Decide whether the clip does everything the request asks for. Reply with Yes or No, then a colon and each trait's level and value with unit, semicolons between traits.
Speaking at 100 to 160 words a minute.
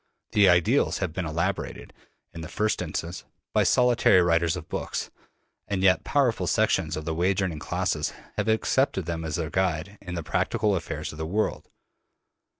No: average, 170 wpm